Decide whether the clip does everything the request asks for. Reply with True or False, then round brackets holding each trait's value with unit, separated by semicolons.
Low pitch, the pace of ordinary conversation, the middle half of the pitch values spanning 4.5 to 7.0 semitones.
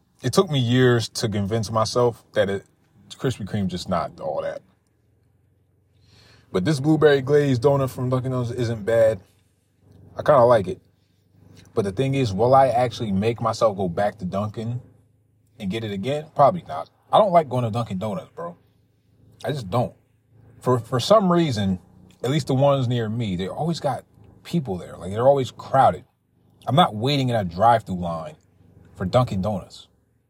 True (115 Hz; 180 wpm; 4.8 semitones)